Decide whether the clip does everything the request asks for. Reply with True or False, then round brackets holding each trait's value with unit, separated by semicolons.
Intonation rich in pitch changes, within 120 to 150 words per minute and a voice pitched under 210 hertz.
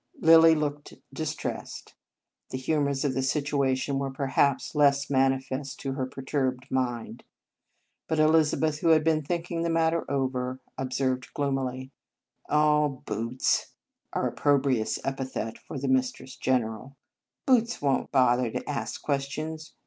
False (2.5 semitones; 135 wpm; 140 Hz)